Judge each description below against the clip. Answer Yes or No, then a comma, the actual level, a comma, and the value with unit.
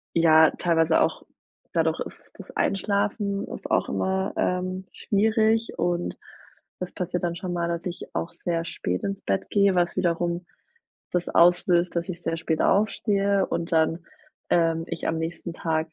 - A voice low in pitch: No, medium, 175 Hz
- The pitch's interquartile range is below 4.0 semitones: Yes, narrow, 2.4 semitones